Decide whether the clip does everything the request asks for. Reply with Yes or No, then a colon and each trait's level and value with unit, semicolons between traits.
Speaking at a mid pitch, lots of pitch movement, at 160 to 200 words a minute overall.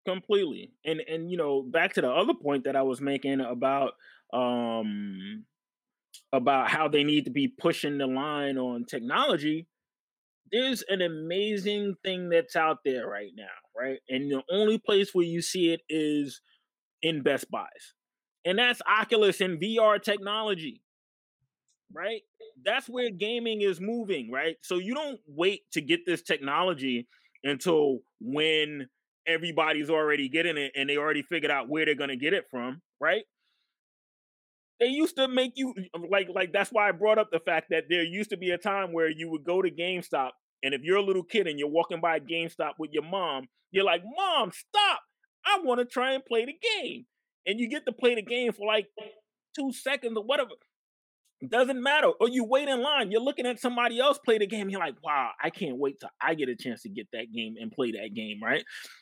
Yes: medium, 180 Hz; wide, 7.3 semitones; average, 195 wpm